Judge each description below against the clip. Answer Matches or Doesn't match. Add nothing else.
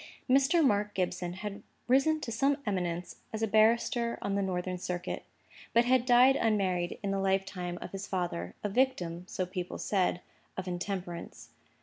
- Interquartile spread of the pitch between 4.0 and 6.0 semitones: Matches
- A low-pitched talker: Doesn't match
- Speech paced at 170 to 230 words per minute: Doesn't match